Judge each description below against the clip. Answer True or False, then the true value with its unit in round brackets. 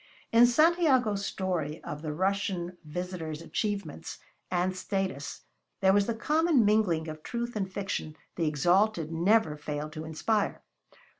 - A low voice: False (185 Hz)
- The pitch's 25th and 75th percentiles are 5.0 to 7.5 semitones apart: True (5.3 semitones)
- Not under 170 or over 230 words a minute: False (135 wpm)